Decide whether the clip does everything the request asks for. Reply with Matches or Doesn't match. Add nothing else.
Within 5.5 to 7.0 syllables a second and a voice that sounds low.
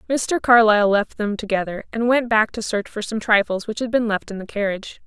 Doesn't match